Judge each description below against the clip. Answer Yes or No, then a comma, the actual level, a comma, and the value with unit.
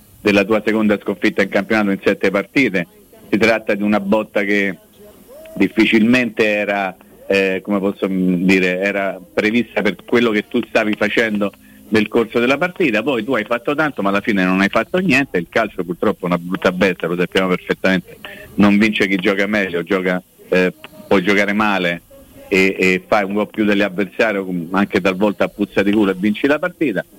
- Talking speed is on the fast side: Yes, fast, 180 wpm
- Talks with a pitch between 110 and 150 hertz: No, low, 100 Hz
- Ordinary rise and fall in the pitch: No, narrow, 2.3 semitones